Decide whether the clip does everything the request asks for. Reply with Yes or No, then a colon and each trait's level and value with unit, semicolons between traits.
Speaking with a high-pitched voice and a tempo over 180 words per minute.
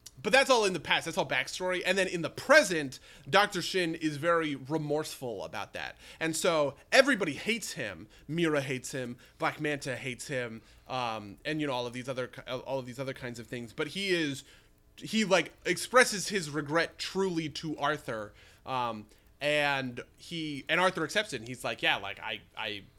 No: medium, 150 Hz; average, 190 wpm